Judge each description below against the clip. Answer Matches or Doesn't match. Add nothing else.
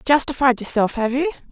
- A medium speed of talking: Matches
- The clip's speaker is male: Doesn't match